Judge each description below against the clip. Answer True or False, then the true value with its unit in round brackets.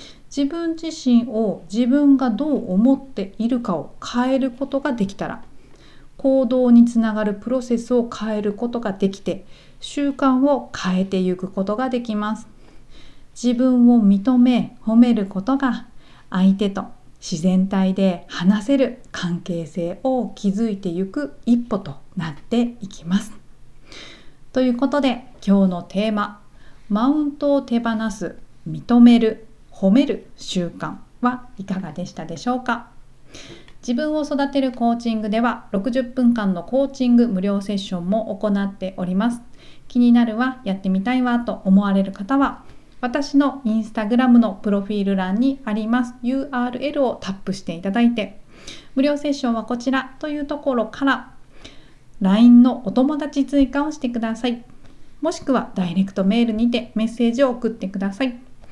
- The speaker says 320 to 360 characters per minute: False (305 characters per minute)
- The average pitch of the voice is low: False (235 Hz)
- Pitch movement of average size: True (4.5 semitones)